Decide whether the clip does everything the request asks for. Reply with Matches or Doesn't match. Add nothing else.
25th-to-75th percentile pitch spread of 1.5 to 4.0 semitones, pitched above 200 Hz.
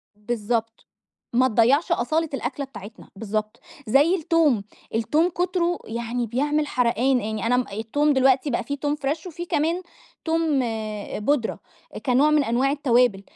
Doesn't match